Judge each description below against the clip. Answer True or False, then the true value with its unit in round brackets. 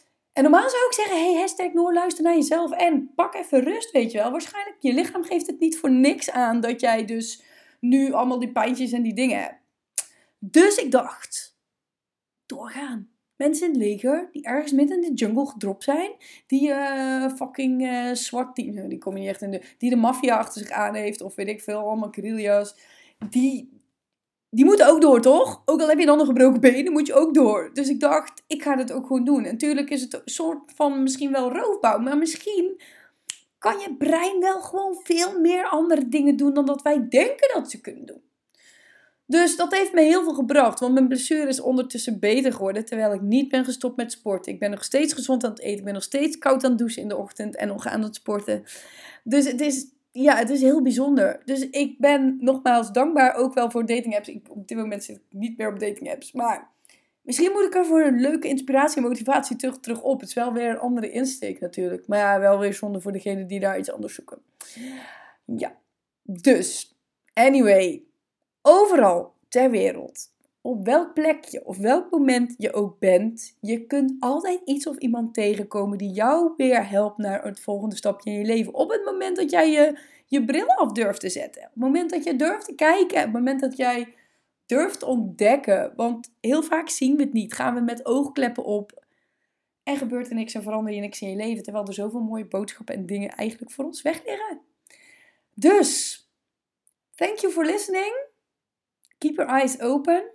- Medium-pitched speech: False (265 Hz)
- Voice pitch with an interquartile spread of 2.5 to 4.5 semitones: False (4.9 semitones)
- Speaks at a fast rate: True (210 wpm)